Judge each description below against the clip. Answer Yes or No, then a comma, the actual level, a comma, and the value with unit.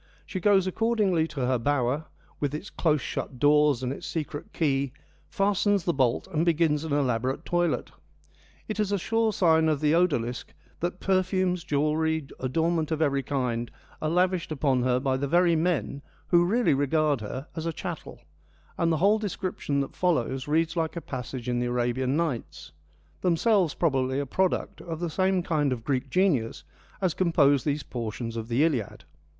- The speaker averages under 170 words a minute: No, average, 175 wpm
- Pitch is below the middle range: No, medium, 155 Hz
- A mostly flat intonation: No, average, 4.8 semitones